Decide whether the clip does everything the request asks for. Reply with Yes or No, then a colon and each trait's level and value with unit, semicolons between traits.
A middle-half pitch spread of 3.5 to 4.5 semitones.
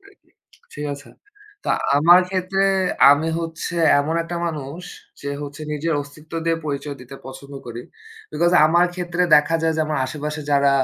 No: average, 2.8 semitones